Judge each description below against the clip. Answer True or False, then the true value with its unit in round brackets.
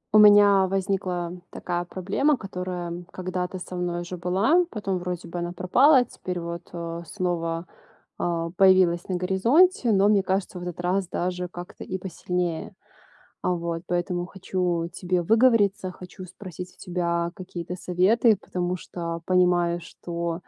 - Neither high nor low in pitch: True (180 Hz)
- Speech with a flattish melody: True (1.7 semitones)